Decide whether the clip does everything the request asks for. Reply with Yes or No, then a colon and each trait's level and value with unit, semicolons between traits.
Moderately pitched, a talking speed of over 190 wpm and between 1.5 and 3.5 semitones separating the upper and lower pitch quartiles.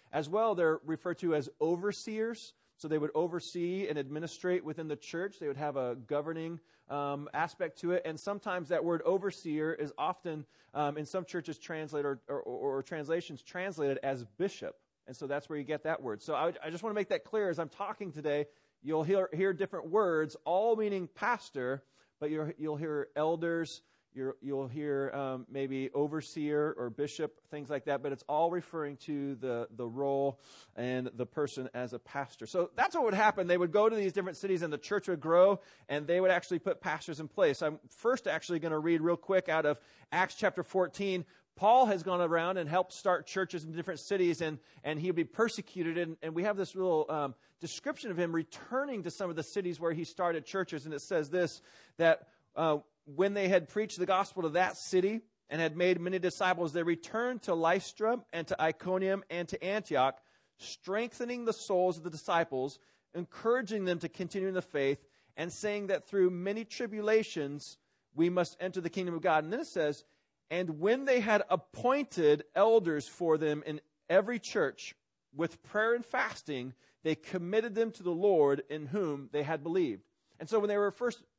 No: medium, 170 Hz; average, 200 wpm; average, 4.3 semitones